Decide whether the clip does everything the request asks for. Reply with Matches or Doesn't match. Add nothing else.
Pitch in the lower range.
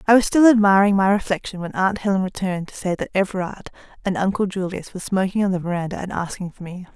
Doesn't match